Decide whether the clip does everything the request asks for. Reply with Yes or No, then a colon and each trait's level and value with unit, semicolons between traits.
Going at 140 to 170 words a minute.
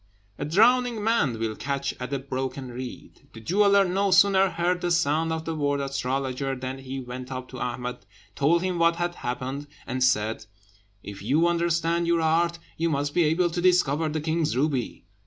No: average, 185 wpm